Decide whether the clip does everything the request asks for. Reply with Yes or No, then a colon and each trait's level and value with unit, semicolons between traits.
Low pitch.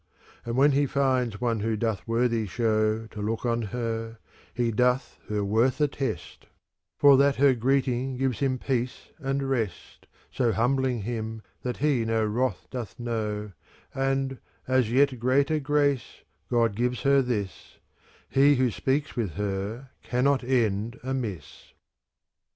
Yes: low, 125 Hz